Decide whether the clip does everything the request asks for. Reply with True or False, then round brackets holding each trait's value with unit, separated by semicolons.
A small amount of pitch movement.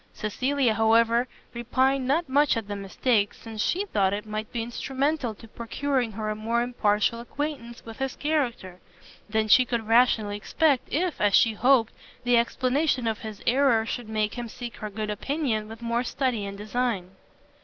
False (3.3 semitones)